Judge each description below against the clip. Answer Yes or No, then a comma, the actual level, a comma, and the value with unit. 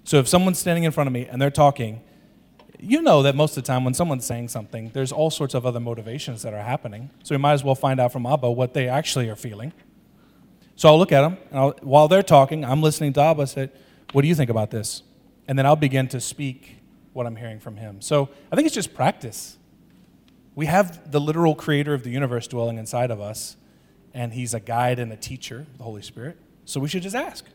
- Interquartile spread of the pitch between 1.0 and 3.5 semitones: No, average, 4.0 semitones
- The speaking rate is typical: No, fast, 240 wpm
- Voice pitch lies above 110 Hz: Yes, low, 135 Hz